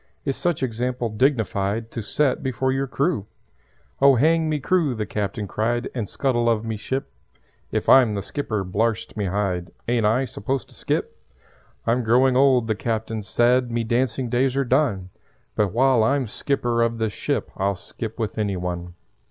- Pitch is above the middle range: No, low, 115 Hz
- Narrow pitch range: No, average, 3.7 semitones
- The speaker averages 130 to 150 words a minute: No, average, 175 wpm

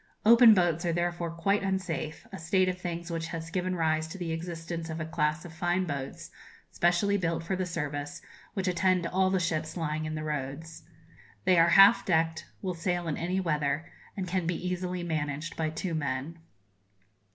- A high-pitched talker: No, medium, 170 Hz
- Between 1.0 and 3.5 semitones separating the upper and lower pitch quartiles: Yes, narrow, 2.4 semitones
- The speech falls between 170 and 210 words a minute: Yes, average, 185 wpm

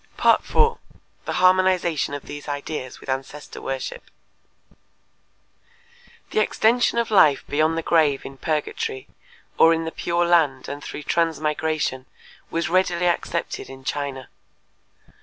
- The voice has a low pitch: No, medium, 160 Hz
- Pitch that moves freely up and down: No, average, 3.5 semitones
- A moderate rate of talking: No, slow, 120 wpm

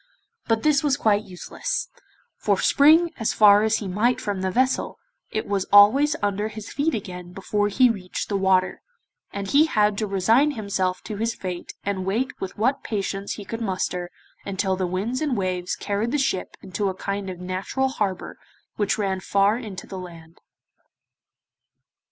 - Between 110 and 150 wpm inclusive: No, average, 175 wpm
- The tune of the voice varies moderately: Yes, average, 3.5 semitones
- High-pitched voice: Yes, high, 205 Hz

